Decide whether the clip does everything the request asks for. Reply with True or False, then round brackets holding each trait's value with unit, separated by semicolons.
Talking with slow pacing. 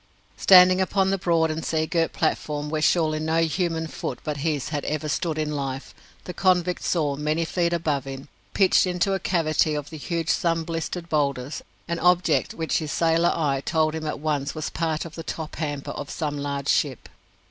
False (195 wpm)